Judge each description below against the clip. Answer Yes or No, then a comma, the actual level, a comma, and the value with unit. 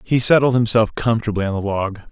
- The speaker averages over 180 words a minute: Yes, average, 200 wpm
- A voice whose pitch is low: Yes, low, 110 Hz